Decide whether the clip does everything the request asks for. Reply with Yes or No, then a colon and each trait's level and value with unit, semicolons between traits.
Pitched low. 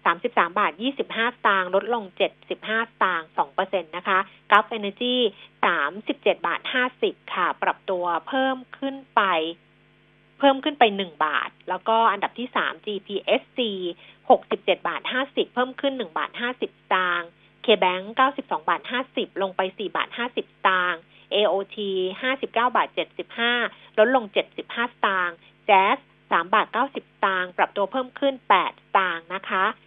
No: high, 210 Hz